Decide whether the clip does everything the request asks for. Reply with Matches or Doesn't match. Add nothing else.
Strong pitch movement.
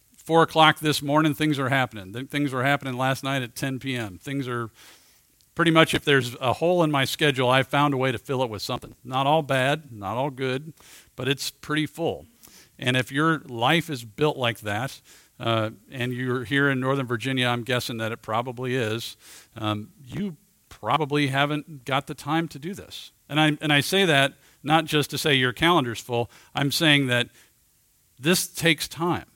Doesn't match